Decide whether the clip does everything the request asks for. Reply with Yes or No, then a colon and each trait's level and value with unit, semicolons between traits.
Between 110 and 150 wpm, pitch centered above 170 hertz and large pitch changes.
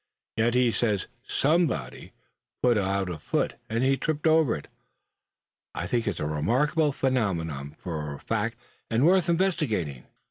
No: average, 145 wpm; low, 115 Hz; wide, 8.9 semitones